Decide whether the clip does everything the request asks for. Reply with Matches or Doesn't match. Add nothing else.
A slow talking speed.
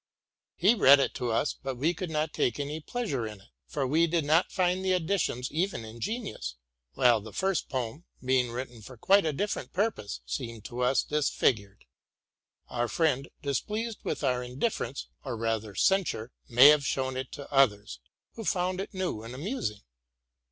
Doesn't match